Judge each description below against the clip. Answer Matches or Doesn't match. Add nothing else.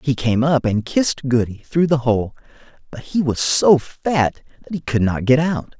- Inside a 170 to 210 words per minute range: Matches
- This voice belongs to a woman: Doesn't match